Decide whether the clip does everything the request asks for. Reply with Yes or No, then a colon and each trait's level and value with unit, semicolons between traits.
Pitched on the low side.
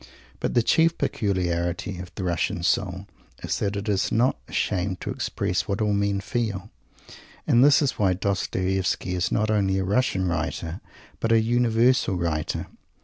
Yes: low, 100 Hz